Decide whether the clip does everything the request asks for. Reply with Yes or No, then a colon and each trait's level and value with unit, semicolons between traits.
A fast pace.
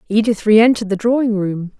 No: average, 165 wpm